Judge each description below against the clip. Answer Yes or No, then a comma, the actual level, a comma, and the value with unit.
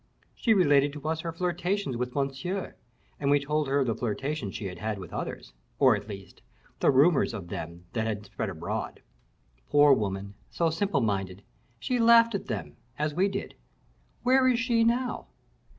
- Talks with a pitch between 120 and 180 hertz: Yes, medium, 140 Hz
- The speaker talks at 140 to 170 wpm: No, average, 180 wpm